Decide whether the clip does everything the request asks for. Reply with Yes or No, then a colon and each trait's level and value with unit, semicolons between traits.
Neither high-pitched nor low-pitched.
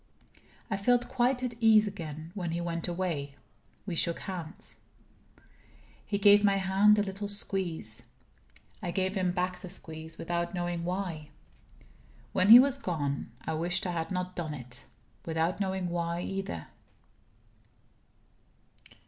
Yes: medium, 180 Hz